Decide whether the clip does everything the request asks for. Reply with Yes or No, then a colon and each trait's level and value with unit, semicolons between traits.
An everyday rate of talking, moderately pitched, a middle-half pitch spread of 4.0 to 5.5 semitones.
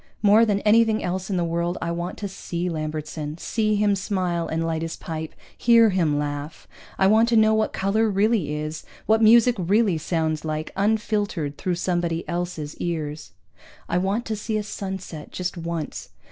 Yes: average, 175 wpm; medium, 180 Hz; average, 4.5 semitones